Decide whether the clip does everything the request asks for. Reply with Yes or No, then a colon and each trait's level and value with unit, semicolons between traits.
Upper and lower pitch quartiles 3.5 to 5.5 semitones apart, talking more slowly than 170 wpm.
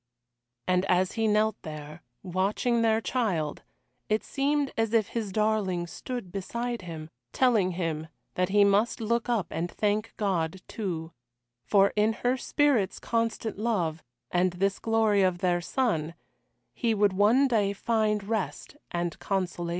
Yes: average, 4.0 semitones; average, 145 wpm